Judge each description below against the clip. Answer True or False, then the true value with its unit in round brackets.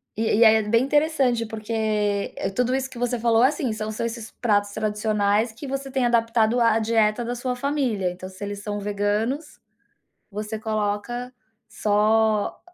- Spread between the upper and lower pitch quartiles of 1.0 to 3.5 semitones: True (2.7 semitones)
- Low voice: False (225 Hz)